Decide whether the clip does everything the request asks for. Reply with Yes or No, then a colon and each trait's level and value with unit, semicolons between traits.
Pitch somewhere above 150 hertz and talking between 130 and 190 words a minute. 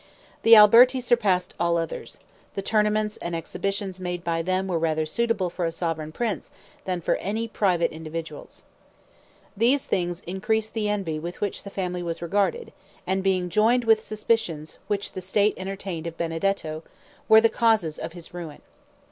Yes: high, 190 Hz; average, 165 wpm